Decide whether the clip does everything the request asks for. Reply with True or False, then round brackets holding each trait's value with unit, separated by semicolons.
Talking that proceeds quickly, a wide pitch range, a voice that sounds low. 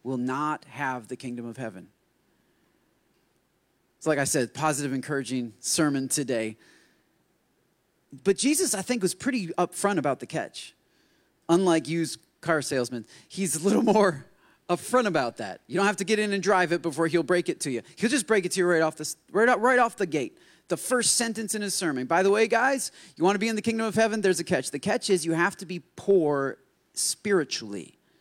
False (210 wpm; 6.3 semitones; 175 Hz)